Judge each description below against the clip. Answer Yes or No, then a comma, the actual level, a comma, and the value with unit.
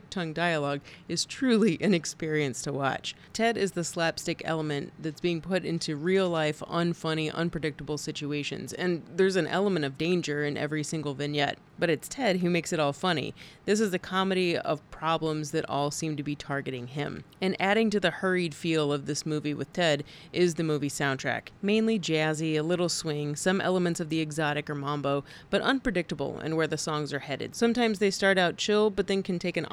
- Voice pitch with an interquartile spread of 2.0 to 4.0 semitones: Yes, average, 3.6 semitones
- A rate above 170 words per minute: Yes, average, 200 wpm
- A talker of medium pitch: Yes, medium, 160 Hz